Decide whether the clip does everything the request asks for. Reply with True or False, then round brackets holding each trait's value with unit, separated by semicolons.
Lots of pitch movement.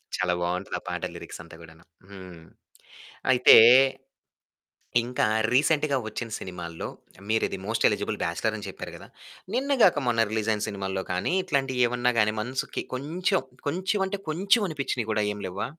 True (6.9 semitones)